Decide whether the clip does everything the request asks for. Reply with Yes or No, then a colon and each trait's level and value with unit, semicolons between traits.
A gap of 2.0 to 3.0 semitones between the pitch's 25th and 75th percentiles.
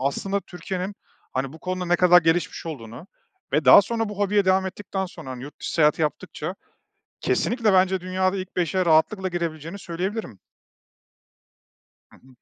No: average, 3.4 semitones